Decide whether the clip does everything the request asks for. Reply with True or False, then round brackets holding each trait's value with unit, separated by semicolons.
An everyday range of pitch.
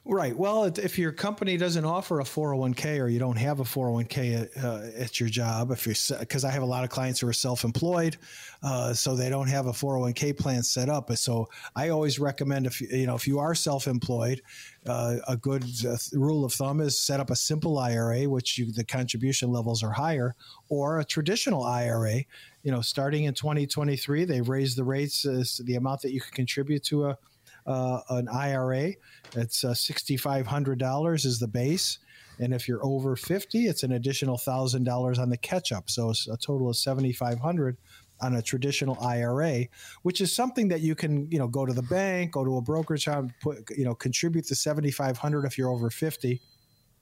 True (3.2 semitones)